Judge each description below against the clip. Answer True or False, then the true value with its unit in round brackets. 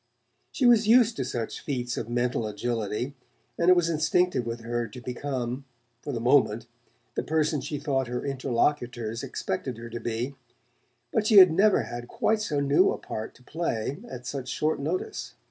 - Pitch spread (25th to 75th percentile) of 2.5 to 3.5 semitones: False (4.8 semitones)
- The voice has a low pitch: True (130 Hz)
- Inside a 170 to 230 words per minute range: True (180 wpm)